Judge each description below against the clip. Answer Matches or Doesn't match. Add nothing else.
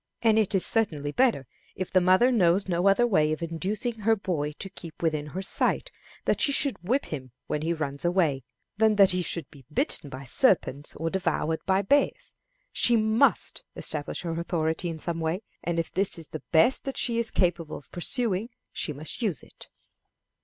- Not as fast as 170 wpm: Doesn't match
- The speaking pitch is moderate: Matches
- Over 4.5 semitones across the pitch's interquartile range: Matches